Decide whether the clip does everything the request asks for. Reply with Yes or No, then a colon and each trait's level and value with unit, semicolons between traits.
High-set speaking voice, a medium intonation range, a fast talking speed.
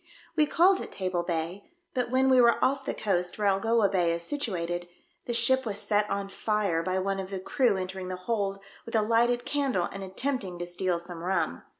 Yes: high, 195 Hz; average, 4.5 semitones; fast, 210 wpm